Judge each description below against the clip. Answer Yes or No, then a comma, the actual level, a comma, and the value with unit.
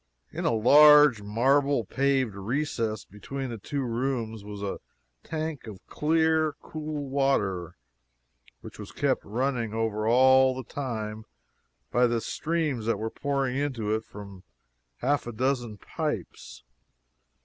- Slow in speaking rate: Yes, slow, 130 wpm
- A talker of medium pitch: No, low, 125 Hz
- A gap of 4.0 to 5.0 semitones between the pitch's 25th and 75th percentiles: Yes, average, 4.5 semitones